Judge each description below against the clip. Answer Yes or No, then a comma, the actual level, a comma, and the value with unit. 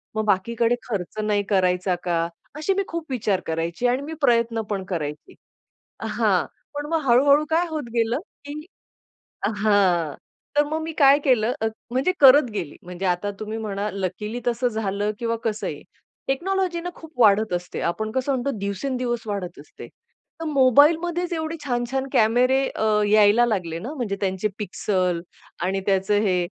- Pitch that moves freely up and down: Yes, wide, 5.8 semitones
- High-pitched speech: Yes, high, 225 Hz